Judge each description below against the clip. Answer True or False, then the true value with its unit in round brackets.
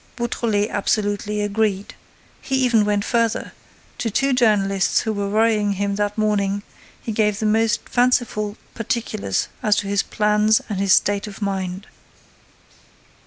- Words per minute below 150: True (140 wpm)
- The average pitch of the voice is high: True (210 Hz)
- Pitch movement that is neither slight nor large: False (1.6 semitones)